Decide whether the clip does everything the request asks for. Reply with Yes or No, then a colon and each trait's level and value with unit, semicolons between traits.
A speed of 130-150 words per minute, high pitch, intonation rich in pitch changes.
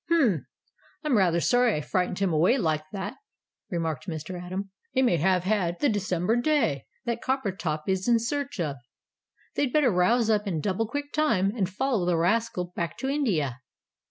No: average, 175 wpm; high, 195 Hz; wide, 5.7 semitones